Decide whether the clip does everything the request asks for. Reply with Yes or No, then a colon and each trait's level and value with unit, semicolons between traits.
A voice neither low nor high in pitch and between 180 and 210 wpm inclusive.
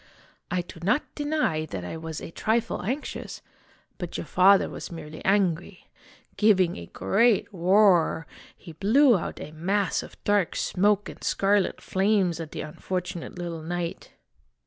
No: medium, 180 Hz; average, 145 wpm